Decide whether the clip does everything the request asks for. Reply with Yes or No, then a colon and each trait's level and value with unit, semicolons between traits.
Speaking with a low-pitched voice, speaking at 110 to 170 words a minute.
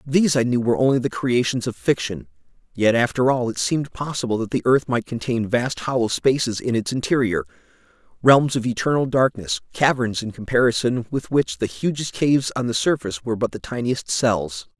No: low, 125 Hz; average, 180 wpm